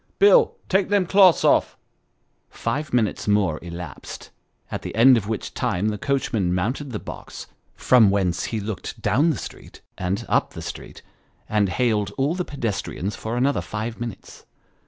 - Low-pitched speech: Yes, low, 110 Hz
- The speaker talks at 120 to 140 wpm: No, average, 165 wpm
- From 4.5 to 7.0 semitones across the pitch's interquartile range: Yes, wide, 5.5 semitones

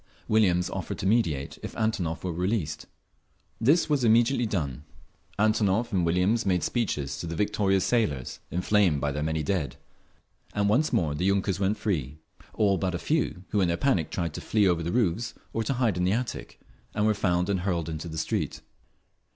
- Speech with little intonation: No, average, 4.6 semitones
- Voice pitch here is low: Yes, very low, 95 Hz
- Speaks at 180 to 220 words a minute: Yes, average, 185 wpm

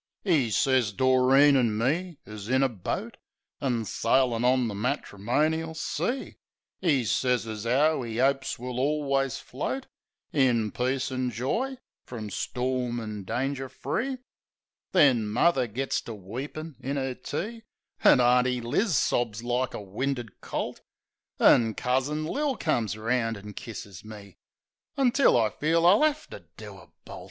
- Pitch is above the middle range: No, low, 130 Hz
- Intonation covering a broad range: No, average, 4.2 semitones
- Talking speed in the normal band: Yes, average, 145 wpm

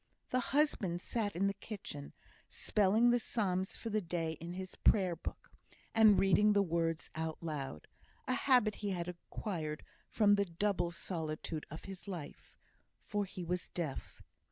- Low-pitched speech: No, medium, 185 Hz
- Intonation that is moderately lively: Yes, average, 3.8 semitones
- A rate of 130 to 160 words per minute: Yes, average, 155 wpm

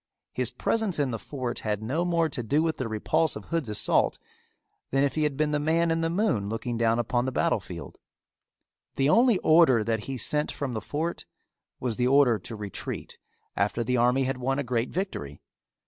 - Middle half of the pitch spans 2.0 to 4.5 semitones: No, wide, 5.4 semitones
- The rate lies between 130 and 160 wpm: No, fast, 205 wpm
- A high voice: No, low, 135 Hz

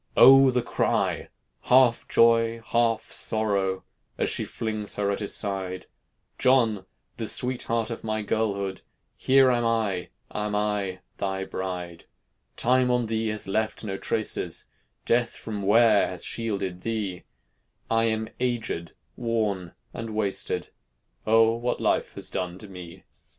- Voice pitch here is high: No, low, 110 Hz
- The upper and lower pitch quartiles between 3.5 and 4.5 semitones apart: No, average, 3.0 semitones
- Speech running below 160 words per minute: Yes, slow, 135 wpm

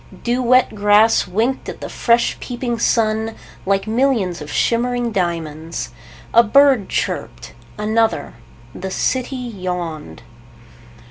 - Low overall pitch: No, high, 220 Hz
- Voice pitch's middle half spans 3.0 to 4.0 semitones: No, average, 4.7 semitones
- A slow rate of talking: Yes, slow, 115 wpm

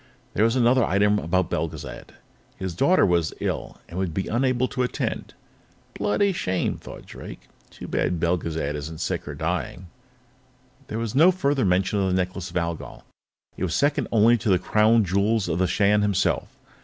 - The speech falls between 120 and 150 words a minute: No, average, 170 wpm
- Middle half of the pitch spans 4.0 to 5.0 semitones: Yes, average, 4.4 semitones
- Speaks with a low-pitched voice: Yes, low, 100 Hz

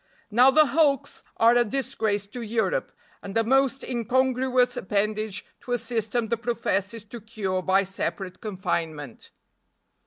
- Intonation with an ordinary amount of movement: Yes, average, 3.6 semitones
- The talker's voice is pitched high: Yes, high, 225 Hz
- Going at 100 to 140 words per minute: Yes, slow, 135 wpm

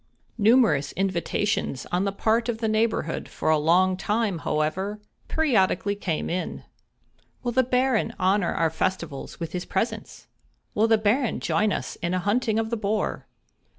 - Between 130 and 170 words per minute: Yes, average, 155 wpm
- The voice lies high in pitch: Yes, high, 205 Hz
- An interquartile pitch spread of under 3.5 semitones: No, average, 4.1 semitones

